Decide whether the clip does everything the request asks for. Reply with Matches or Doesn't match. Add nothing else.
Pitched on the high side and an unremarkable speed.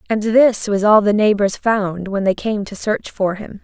Doesn't match